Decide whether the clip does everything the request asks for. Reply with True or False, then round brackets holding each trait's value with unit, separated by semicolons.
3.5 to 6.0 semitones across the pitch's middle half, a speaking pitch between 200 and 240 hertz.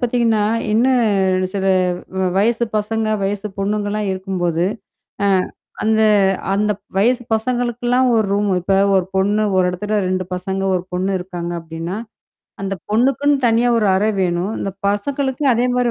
True (3.8 semitones; 210 Hz)